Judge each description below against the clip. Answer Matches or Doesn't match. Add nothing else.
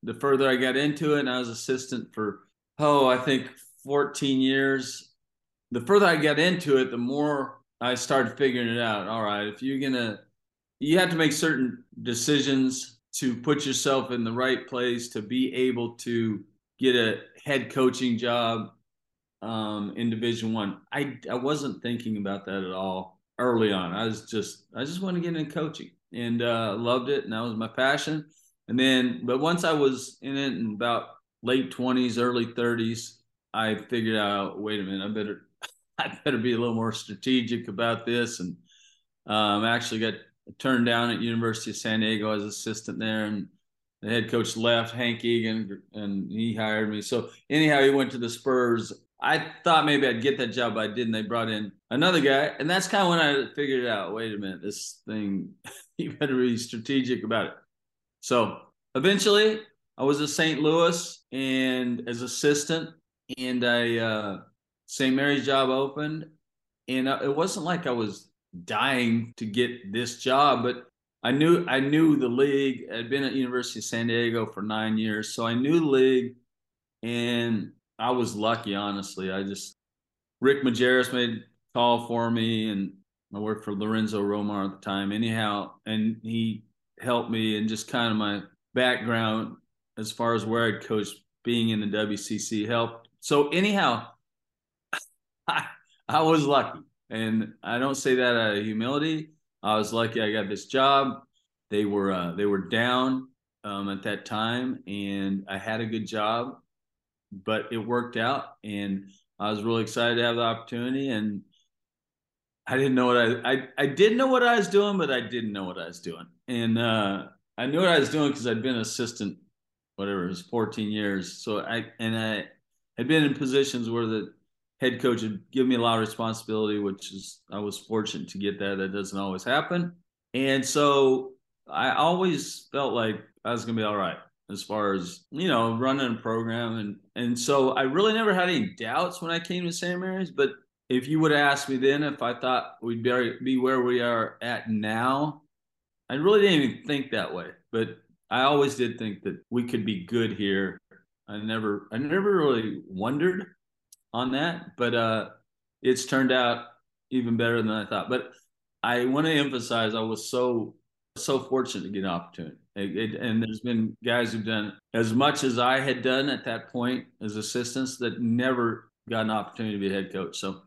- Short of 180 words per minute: Doesn't match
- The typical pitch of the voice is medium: Doesn't match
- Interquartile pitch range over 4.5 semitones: Doesn't match